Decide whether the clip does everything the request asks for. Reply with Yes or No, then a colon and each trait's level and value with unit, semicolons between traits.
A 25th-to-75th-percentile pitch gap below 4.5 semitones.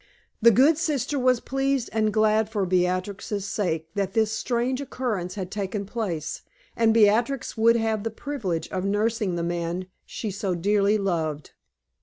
Yes: average, 3.8 semitones